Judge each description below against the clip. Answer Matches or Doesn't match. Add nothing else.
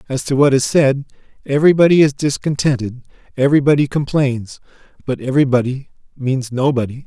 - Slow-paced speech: Matches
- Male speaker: Matches